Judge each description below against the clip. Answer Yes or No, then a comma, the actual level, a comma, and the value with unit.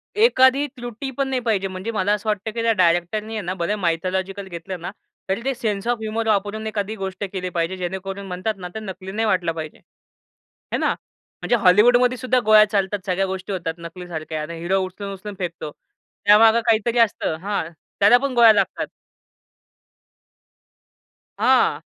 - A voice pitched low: No, high, 200 Hz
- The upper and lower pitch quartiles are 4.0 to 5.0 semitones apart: No, average, 3.3 semitones